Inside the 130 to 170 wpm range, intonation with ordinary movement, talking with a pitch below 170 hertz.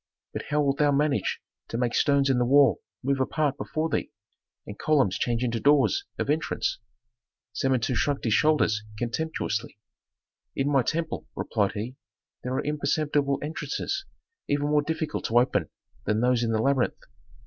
Yes: average, 160 wpm; average, 3.6 semitones; medium, 140 Hz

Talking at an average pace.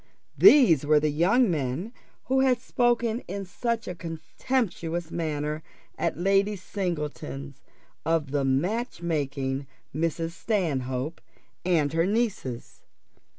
No: slow, 110 wpm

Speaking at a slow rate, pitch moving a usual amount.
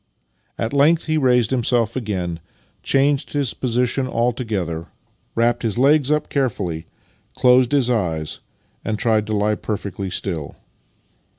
Yes: slow, 125 wpm; average, 4.4 semitones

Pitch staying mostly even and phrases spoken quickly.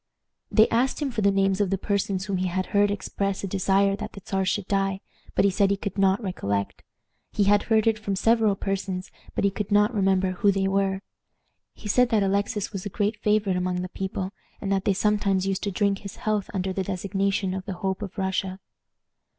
Yes: narrow, 1.3 semitones; fast, 220 wpm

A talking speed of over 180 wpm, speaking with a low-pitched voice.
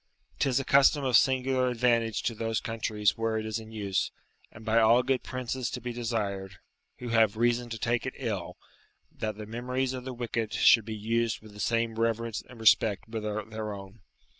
Yes: average, 195 wpm; low, 115 Hz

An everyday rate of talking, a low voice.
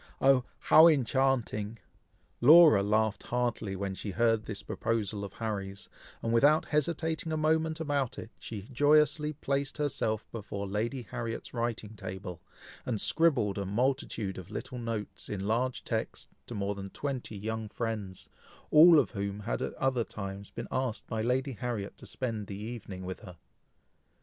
Yes: average, 155 wpm; low, 115 Hz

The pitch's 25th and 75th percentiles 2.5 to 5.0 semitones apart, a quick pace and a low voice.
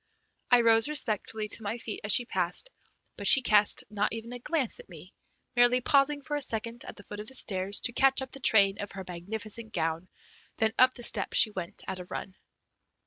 No: average, 3.6 semitones; fast, 215 wpm; high, 225 Hz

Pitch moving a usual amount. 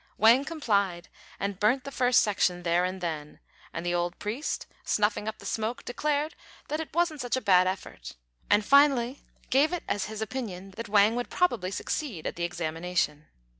No: wide, 6.3 semitones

